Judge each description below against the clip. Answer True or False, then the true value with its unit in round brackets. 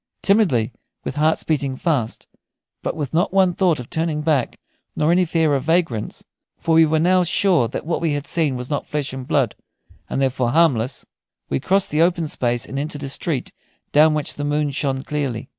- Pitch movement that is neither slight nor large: True (3.8 semitones)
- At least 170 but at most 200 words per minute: True (195 wpm)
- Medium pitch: True (150 Hz)